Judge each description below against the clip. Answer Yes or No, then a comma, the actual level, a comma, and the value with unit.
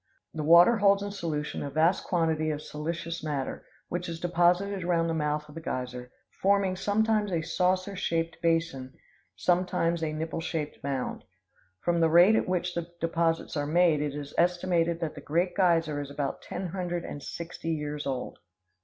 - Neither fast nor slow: Yes, average, 170 wpm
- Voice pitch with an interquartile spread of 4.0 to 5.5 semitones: No, average, 2.7 semitones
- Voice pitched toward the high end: No, medium, 165 Hz